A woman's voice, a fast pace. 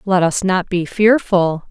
No: female; average, 175 wpm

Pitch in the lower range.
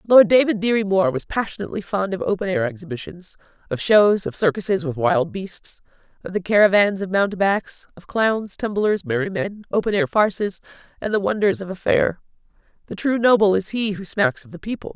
No: high, 190 Hz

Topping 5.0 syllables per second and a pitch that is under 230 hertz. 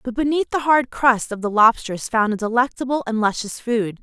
No: 5.4 syllables/s; high, 235 Hz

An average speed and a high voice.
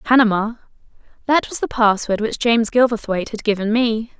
Yes: average, 145 wpm; high, 225 Hz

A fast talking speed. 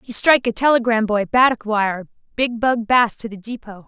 No: average, 185 wpm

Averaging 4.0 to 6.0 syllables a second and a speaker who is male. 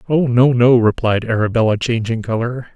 Yes: 5.2 syllables/s; male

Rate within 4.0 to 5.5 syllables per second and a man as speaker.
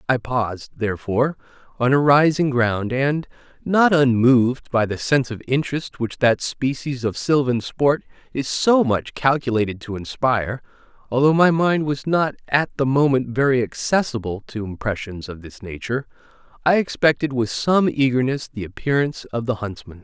No: 3.7 syllables/s; male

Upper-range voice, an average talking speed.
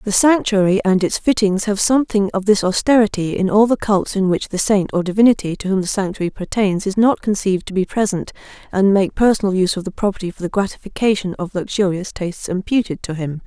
No: high, 195 Hz; fast, 210 wpm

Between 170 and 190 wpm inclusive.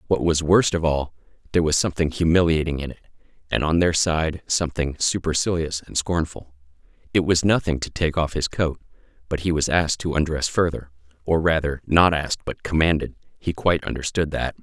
Yes: average, 180 wpm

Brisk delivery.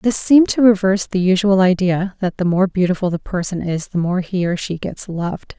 Yes: fast, 225 wpm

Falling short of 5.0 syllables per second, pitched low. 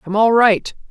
No: 4.5 syllables/s; high, 210 Hz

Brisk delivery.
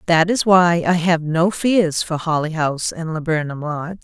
No: average, 195 wpm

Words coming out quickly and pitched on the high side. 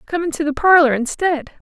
No: average, 175 wpm; very high, 310 Hz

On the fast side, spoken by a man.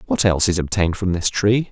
Yes: fast, 245 wpm; male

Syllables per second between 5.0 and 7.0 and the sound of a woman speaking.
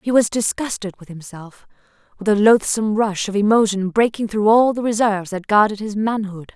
Yes: 5.5 syllables/s; female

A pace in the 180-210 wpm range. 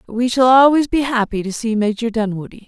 Yes: average, 200 wpm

